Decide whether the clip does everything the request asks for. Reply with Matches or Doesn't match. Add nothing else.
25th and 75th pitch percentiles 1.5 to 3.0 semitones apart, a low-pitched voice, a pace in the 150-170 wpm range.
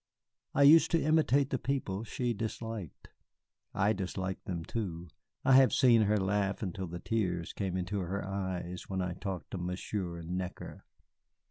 Doesn't match